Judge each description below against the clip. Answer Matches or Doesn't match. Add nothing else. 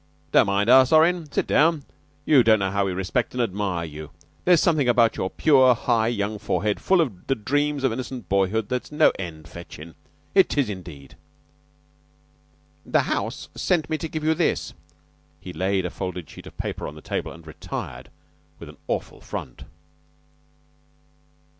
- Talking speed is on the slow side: Doesn't match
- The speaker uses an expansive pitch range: Matches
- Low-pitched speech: Matches